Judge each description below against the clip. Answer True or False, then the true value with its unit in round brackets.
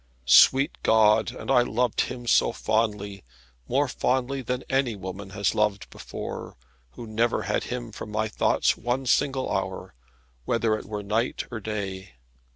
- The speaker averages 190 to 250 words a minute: False (155 wpm)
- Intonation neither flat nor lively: True (3.2 semitones)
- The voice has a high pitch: False (110 Hz)